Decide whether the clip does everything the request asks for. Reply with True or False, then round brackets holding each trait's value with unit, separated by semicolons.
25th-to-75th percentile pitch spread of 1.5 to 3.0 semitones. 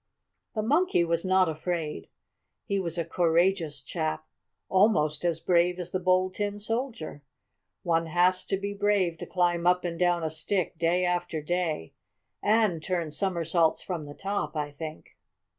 True (2.7 semitones)